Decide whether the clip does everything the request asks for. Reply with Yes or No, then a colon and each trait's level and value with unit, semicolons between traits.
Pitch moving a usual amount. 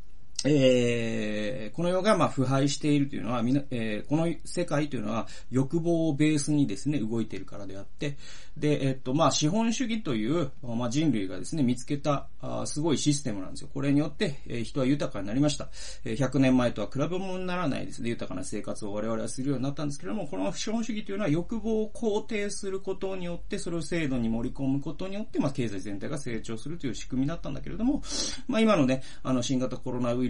No: wide, 5.7 semitones